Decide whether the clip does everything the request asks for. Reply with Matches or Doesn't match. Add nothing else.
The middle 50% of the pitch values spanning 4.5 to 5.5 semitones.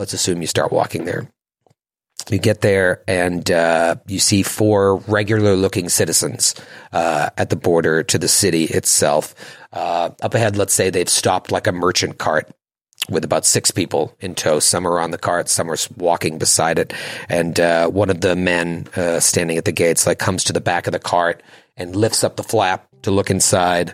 Doesn't match